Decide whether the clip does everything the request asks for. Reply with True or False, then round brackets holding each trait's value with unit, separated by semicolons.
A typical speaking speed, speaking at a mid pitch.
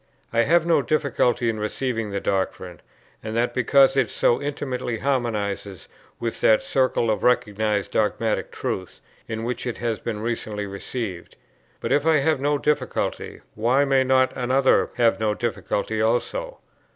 False (150 wpm; 120 Hz)